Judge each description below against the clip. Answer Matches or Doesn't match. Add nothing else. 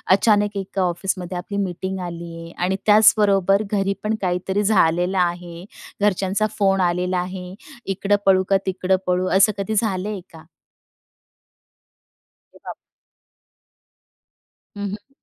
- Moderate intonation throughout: Doesn't match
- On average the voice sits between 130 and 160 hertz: Doesn't match